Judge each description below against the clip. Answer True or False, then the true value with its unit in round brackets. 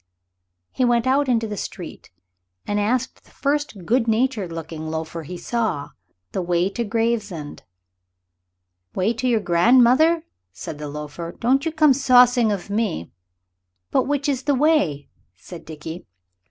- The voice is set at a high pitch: True (225 Hz)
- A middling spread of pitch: False (7.1 semitones)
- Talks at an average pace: True (145 wpm)